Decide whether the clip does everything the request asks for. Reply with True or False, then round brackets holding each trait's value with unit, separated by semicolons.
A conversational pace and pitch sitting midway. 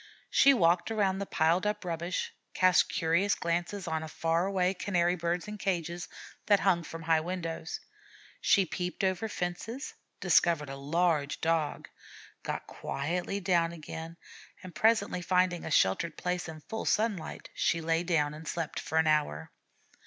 True (150 wpm; 170 Hz)